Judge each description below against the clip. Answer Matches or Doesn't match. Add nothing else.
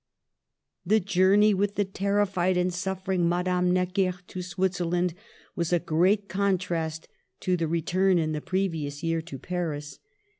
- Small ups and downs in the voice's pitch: Matches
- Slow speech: Doesn't match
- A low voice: Doesn't match